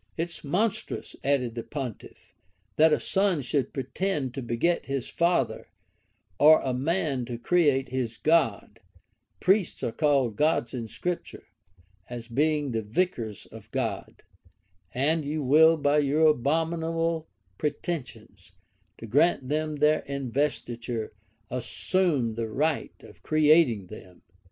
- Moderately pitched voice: Yes, medium, 145 Hz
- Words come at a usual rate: No, slow, 130 wpm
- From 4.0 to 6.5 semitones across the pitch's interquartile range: Yes, average, 5.0 semitones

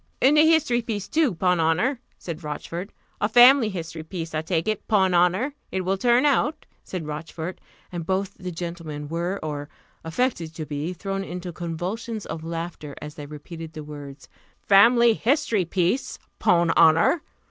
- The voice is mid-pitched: Yes, medium, 175 Hz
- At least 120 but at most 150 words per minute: No, average, 165 wpm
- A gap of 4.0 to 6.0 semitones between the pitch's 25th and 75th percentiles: Yes, average, 5.1 semitones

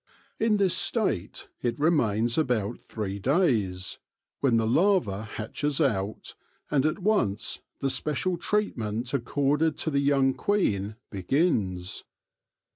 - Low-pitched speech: Yes, low, 130 Hz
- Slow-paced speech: Yes, slow, 120 wpm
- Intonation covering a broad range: Yes, wide, 6.8 semitones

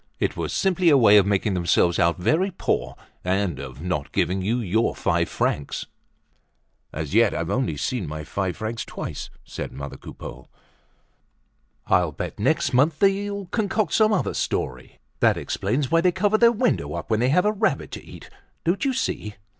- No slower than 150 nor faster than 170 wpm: No, average, 180 wpm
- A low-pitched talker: Yes, low, 115 Hz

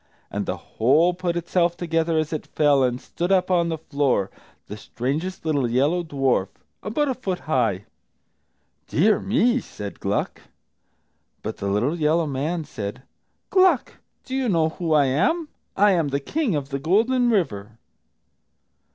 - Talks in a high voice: No, medium, 160 Hz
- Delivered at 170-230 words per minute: No, average, 155 wpm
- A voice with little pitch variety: No, wide, 5.5 semitones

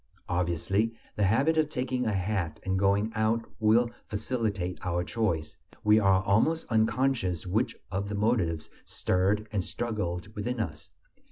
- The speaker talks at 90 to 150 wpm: Yes, average, 145 wpm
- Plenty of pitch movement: No, average, 3.7 semitones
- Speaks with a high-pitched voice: No, low, 105 Hz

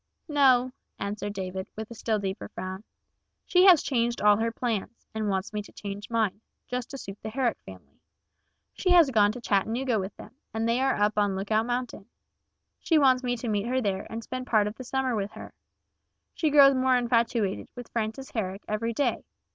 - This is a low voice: No, high, 230 Hz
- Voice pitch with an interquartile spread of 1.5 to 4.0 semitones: Yes, average, 3.6 semitones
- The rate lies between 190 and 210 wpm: Yes, average, 195 wpm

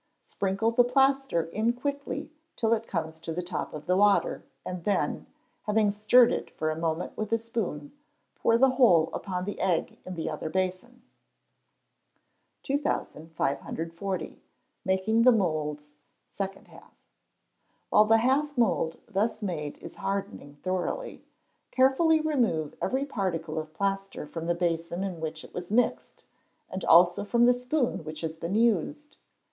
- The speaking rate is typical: Yes, average, 150 wpm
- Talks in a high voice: Yes, high, 195 Hz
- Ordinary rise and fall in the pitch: No, wide, 6.3 semitones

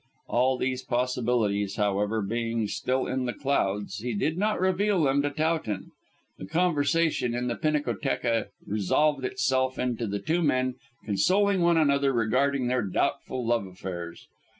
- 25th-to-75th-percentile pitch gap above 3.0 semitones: Yes, average, 4.7 semitones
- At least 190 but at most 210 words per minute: No, average, 145 wpm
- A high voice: No, low, 130 Hz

